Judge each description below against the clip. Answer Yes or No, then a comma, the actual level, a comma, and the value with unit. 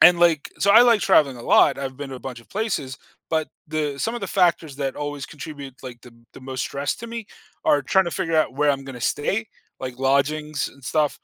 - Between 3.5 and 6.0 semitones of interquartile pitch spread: Yes, average, 4.1 semitones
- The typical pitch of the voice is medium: Yes, medium, 145 Hz